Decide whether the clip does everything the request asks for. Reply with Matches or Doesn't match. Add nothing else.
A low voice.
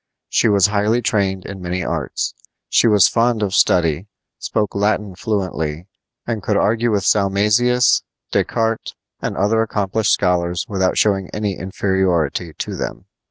Matches